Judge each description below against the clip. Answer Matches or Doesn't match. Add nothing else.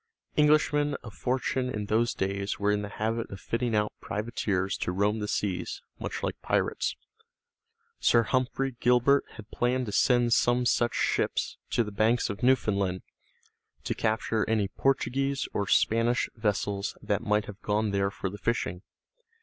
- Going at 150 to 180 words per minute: Matches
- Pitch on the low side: Matches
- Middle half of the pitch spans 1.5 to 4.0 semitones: Matches